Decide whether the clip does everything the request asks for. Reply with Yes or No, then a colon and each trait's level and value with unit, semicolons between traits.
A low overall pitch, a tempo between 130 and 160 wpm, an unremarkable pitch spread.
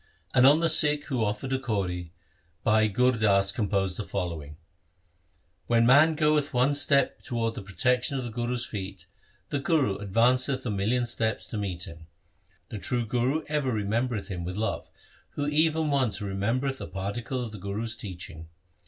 No: low, 115 Hz; average, 170 wpm; average, 5.0 semitones